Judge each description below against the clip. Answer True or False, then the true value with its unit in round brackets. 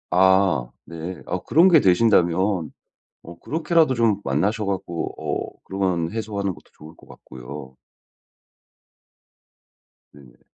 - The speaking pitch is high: False (95 Hz)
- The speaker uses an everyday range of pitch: True (4.5 semitones)